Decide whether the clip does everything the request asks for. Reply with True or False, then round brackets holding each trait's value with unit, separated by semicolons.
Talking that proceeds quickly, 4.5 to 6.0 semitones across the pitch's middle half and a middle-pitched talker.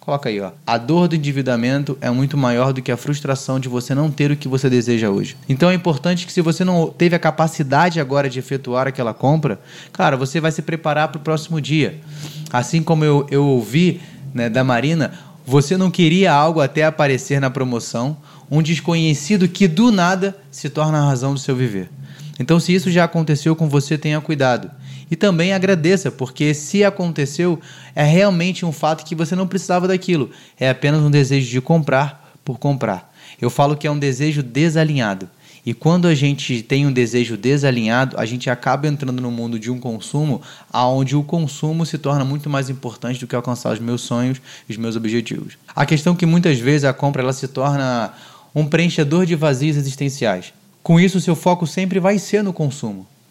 False (195 wpm; 3.9 semitones; 145 Hz)